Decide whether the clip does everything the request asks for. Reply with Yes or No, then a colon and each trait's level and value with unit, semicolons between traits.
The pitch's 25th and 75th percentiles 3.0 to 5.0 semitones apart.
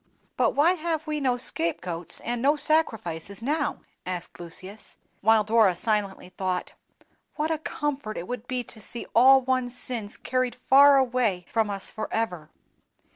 No: wide, 5.5 semitones